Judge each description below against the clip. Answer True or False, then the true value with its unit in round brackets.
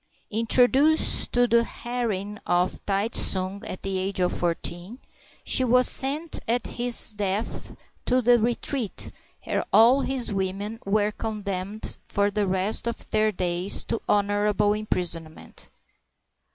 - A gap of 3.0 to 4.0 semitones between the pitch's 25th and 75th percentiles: True (3.6 semitones)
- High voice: True (210 Hz)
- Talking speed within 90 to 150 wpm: True (140 wpm)